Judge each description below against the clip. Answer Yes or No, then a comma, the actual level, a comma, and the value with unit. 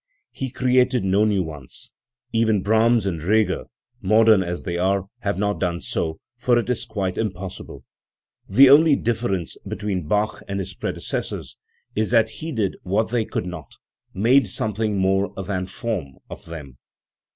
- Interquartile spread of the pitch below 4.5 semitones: Yes, average, 3.6 semitones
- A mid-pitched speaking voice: No, low, 105 Hz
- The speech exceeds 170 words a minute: No, average, 155 wpm